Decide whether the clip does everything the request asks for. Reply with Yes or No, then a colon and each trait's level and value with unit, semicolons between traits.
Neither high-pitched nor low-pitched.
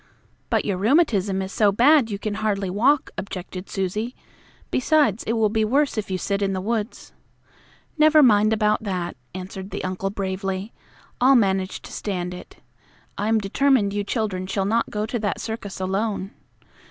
No: high, 205 Hz